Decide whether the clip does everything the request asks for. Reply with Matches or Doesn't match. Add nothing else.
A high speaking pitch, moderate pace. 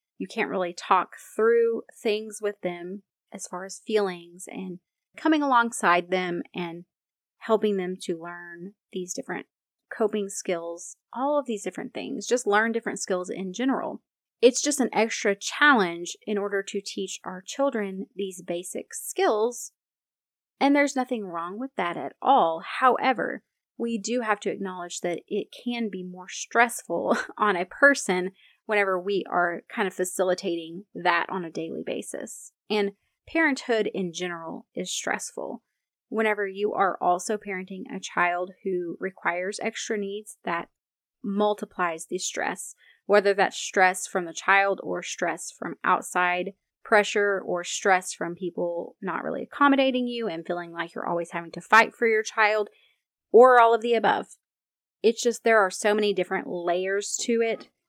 Matches